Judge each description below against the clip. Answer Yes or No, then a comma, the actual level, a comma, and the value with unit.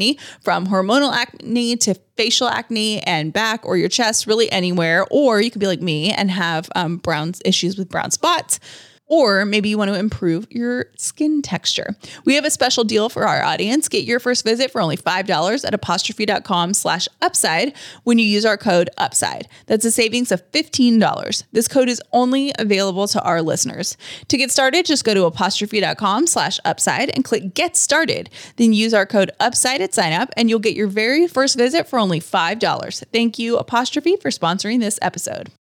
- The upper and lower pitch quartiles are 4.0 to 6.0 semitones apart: Yes, average, 4.4 semitones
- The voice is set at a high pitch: Yes, high, 220 Hz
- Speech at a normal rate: Yes, average, 180 wpm